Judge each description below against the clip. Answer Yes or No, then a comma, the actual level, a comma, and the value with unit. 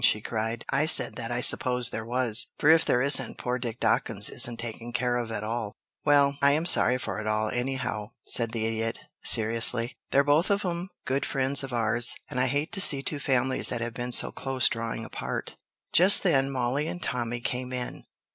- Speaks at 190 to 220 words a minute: Yes, fast, 205 wpm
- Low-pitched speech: Yes, low, 125 Hz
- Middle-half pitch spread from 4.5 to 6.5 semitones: No, average, 3.2 semitones